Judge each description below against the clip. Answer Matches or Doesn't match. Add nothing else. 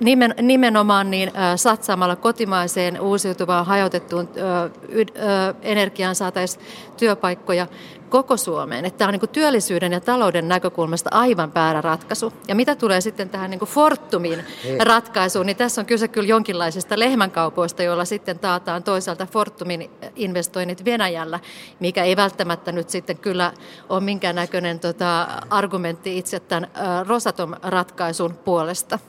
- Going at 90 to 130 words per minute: Matches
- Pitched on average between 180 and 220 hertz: Matches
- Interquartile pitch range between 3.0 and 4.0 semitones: Matches